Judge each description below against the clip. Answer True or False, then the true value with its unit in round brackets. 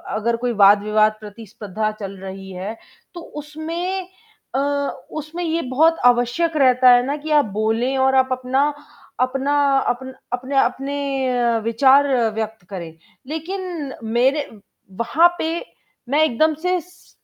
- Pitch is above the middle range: True (265 Hz)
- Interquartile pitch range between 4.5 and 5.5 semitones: True (5.1 semitones)